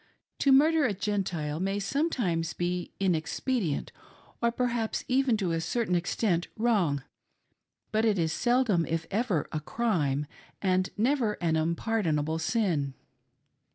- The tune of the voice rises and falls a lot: Yes, wide, 6.2 semitones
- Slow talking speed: Yes, slow, 125 wpm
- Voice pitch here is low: No, high, 195 Hz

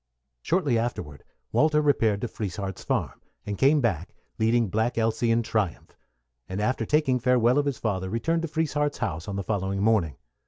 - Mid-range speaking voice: No, low, 115 Hz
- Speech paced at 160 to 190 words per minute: Yes, average, 170 wpm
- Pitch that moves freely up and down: No, average, 5.0 semitones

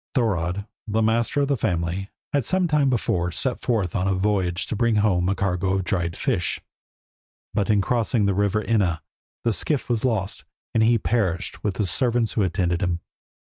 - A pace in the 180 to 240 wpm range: Yes, average, 185 wpm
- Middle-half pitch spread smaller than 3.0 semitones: No, average, 4.2 semitones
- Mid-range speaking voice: No, low, 105 Hz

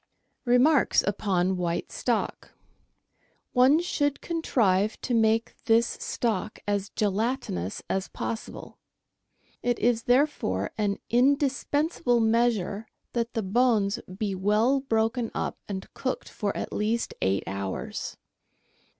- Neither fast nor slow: No, slow, 115 wpm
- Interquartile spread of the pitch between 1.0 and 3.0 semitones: No, average, 3.8 semitones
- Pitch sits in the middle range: No, high, 225 Hz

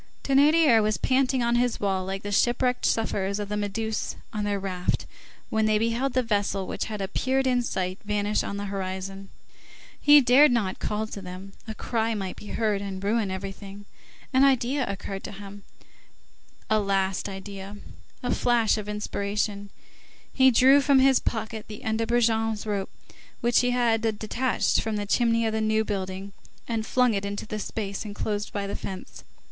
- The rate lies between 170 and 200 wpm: Yes, average, 175 wpm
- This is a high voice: Yes, high, 215 Hz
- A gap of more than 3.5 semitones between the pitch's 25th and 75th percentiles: No, average, 3.1 semitones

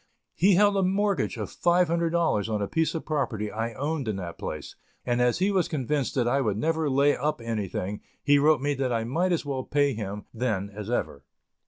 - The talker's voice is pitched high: No, medium, 140 Hz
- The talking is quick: Yes, fast, 220 wpm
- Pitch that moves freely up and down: Yes, wide, 6.4 semitones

